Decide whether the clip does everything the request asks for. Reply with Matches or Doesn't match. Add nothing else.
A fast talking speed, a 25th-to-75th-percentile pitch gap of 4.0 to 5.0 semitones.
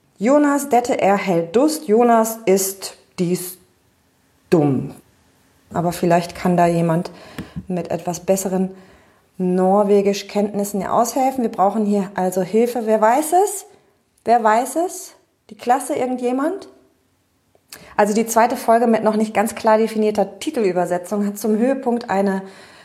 Doesn't match